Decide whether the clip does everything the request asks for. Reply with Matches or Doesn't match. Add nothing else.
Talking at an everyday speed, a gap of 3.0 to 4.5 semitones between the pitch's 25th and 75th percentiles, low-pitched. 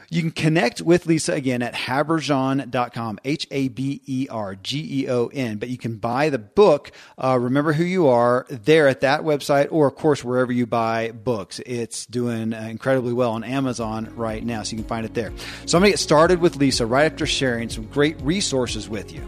Matches